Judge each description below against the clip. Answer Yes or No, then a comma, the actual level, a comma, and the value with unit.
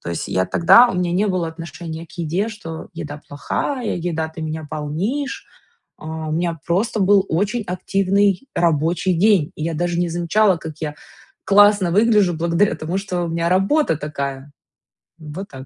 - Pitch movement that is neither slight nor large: Yes, average, 3.7 semitones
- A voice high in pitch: No, medium, 175 Hz